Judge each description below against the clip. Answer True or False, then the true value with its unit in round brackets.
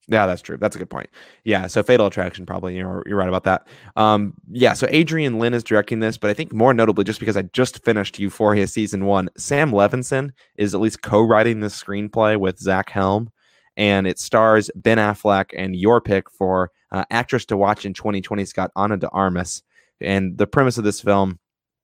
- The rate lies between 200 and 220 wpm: True (205 wpm)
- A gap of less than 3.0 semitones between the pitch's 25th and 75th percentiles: True (2.5 semitones)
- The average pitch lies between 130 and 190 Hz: False (105 Hz)